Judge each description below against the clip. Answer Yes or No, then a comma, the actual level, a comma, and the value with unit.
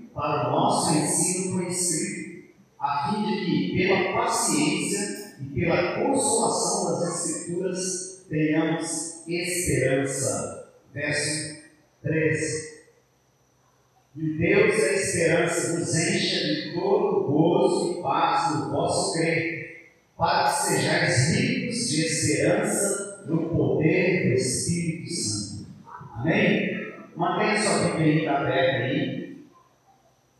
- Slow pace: Yes, slow, 105 wpm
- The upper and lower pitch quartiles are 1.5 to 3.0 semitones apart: Yes, narrow, 2.5 semitones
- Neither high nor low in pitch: Yes, medium, 165 Hz